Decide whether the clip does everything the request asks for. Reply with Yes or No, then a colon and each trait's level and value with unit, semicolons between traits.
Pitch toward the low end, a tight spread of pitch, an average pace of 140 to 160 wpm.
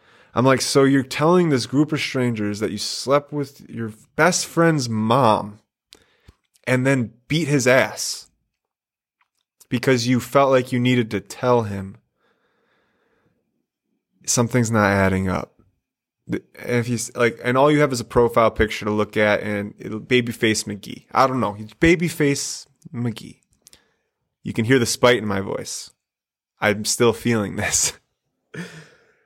No: low, 120 Hz; average, 4.1 semitones; average, 150 wpm